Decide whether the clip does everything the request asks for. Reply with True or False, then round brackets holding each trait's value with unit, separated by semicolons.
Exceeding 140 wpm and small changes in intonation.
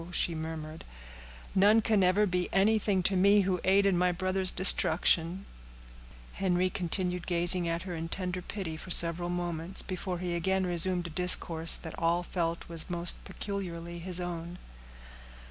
True (155 wpm; 1.8 semitones)